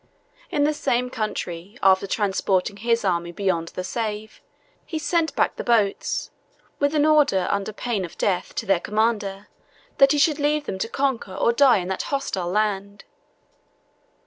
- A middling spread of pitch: No, wide, 6.2 semitones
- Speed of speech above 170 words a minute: No, average, 165 wpm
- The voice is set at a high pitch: Yes, high, 215 Hz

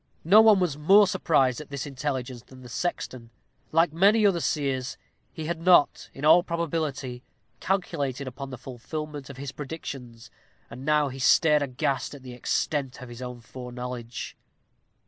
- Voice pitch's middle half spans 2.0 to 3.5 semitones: No, average, 4.2 semitones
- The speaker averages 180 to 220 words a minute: No, average, 160 wpm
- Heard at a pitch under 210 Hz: Yes, medium, 140 Hz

